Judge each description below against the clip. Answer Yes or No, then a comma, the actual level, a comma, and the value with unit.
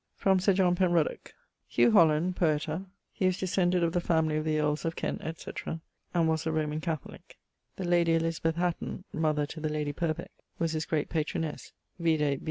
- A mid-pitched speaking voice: Yes, medium, 160 Hz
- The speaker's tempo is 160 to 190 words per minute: Yes, average, 185 wpm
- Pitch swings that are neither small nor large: No, narrow, 2.1 semitones